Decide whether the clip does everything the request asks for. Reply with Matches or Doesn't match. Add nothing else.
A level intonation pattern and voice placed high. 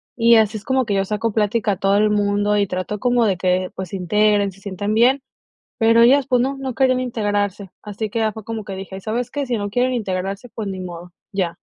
Doesn't match